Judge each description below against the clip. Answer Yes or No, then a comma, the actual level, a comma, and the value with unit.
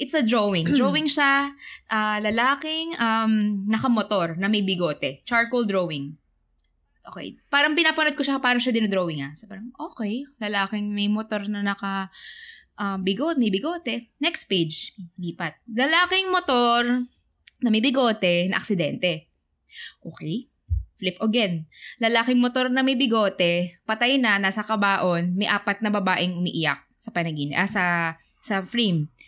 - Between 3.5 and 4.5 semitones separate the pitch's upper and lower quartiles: No, average, 5.2 semitones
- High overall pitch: Yes, high, 215 Hz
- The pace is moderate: Yes, average, 140 wpm